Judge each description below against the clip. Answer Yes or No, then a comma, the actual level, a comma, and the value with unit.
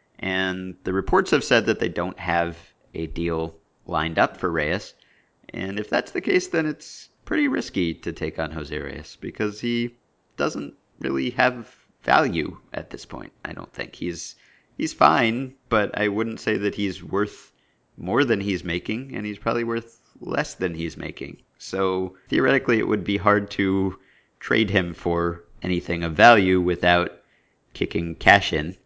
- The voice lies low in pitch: Yes, very low, 95 Hz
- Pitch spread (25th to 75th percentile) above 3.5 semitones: Yes, average, 4.2 semitones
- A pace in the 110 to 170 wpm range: Yes, average, 165 wpm